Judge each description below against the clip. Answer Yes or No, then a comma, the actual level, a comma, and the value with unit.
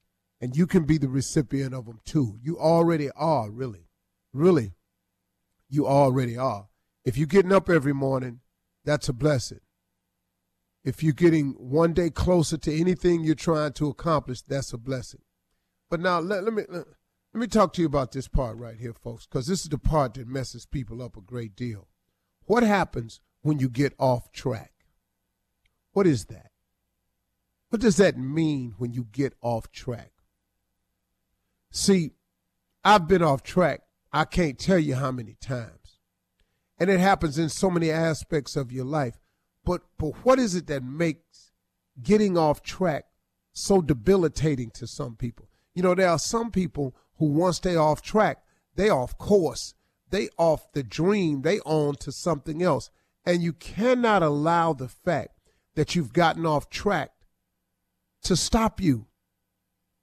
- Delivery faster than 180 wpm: No, average, 165 wpm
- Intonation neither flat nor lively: No, wide, 7.9 semitones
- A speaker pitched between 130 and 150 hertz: Yes, medium, 140 Hz